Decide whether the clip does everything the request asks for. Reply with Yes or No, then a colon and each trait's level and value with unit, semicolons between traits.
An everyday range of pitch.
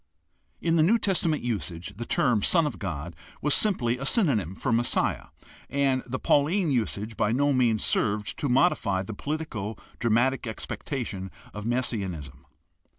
No: wide, 5.8 semitones